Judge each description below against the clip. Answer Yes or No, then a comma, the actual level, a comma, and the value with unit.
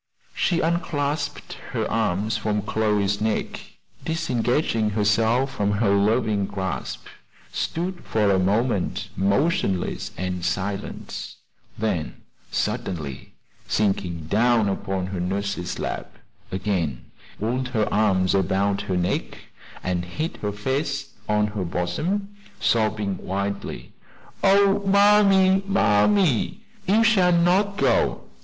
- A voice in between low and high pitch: No, low, 105 Hz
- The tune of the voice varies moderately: No, wide, 8.0 semitones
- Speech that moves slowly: Yes, slow, 110 wpm